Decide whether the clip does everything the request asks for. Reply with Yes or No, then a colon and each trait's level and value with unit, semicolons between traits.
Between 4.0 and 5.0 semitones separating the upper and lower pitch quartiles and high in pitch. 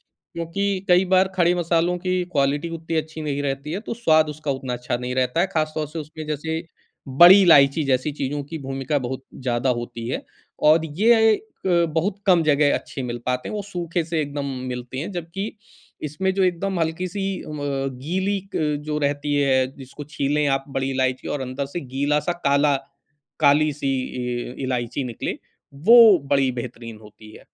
No: average, 4.4 semitones; medium, 150 Hz